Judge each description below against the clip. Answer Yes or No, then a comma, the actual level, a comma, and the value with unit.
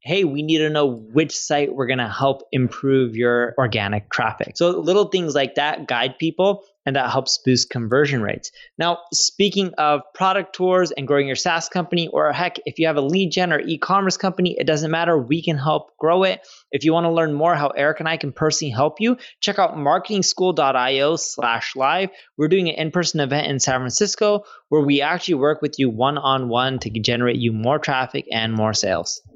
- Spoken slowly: No, average, 195 wpm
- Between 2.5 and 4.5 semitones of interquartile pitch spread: No, average, 5.0 semitones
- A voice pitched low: No, medium, 155 Hz